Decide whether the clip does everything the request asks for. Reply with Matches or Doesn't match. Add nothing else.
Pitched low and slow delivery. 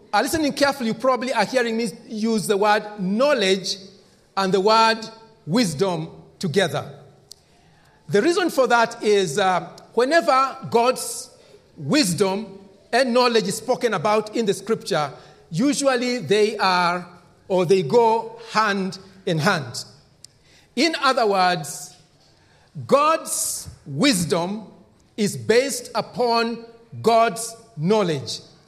Doesn't match